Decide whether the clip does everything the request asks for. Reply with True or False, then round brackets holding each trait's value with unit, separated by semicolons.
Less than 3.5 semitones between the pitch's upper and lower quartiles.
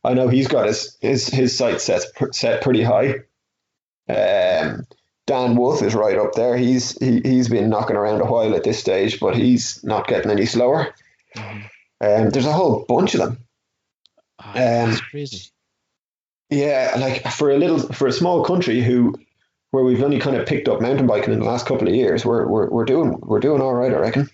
True (2.9 semitones)